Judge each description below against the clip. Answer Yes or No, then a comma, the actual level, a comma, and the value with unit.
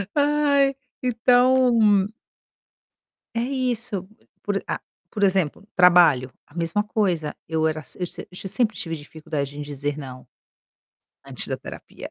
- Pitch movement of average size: No, wide, 7.7 semitones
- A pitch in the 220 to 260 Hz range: No, medium, 185 Hz